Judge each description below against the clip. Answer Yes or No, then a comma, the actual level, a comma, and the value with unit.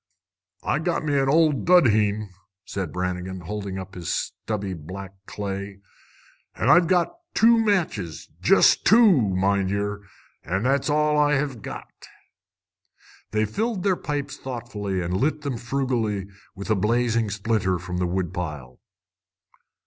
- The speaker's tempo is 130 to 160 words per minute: Yes, slow, 135 wpm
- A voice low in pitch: Yes, low, 105 Hz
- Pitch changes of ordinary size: No, wide, 7.5 semitones